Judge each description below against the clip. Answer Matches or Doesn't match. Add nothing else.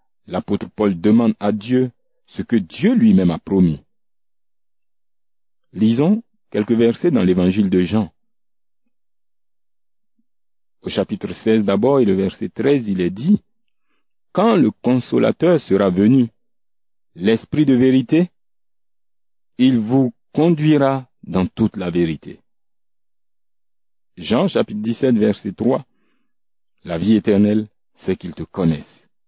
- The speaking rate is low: Matches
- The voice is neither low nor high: Doesn't match